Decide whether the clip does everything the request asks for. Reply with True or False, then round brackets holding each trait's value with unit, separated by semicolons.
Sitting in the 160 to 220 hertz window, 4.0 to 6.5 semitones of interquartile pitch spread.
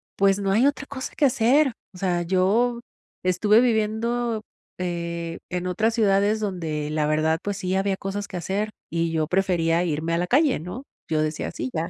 True (190 Hz; 4.6 semitones)